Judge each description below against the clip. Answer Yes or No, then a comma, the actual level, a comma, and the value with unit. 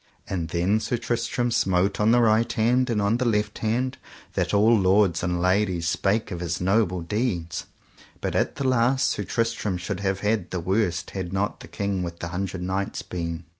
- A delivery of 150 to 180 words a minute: No, average, 195 wpm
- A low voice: Yes, low, 100 Hz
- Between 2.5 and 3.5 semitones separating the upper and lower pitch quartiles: No, average, 4.0 semitones